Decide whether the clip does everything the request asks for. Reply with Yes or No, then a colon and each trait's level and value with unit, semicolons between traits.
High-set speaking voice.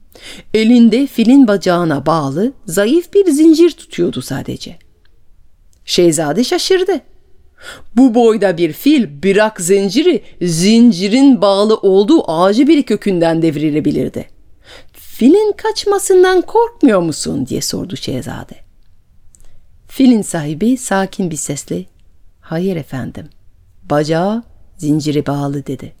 Yes: high, 200 Hz